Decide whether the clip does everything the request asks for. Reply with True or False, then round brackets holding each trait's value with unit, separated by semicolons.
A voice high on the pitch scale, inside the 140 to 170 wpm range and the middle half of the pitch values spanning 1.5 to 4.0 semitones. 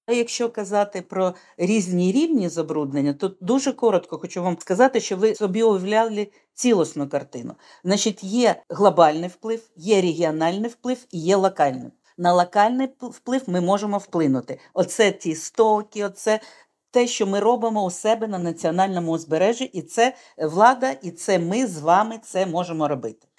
False (200 Hz; 150 wpm; 4.5 semitones)